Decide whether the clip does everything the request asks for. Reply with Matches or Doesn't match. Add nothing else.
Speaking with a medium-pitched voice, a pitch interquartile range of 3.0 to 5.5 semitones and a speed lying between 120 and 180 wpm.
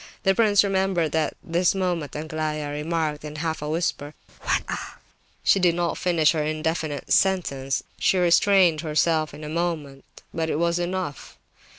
Doesn't match